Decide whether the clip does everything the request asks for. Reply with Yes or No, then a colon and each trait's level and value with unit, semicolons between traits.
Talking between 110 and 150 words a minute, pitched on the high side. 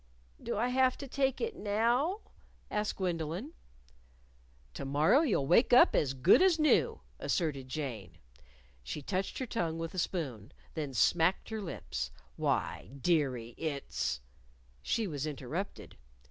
No: average, 140 wpm; medium, 165 Hz